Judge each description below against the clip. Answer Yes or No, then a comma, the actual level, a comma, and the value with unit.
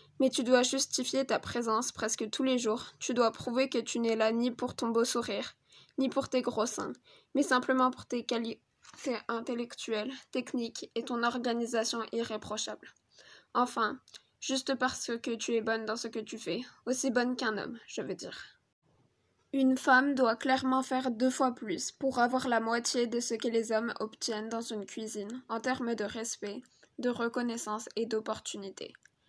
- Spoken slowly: No, average, 175 wpm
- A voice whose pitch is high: Yes, high, 240 Hz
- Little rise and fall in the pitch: Yes, narrow, 2.3 semitones